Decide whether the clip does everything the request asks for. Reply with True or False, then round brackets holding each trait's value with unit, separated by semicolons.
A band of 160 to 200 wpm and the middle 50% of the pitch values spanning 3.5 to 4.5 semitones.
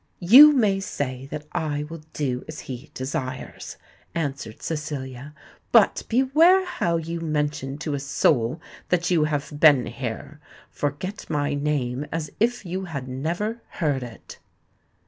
False (140 wpm; 3.9 semitones)